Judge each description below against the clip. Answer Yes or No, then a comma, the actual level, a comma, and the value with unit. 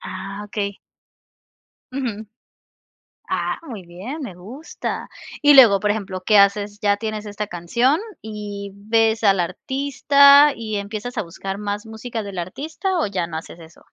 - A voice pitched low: No, high, 210 Hz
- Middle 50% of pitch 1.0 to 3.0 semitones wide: No, average, 3.6 semitones